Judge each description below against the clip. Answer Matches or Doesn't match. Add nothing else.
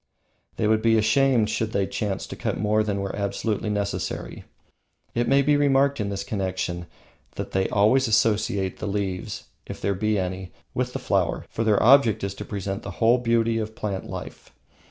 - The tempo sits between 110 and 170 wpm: Doesn't match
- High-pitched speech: Doesn't match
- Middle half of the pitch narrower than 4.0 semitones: Matches